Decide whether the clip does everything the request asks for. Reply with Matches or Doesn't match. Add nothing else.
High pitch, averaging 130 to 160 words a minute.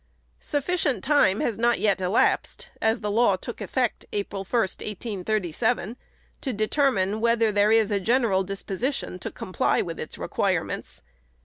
Matches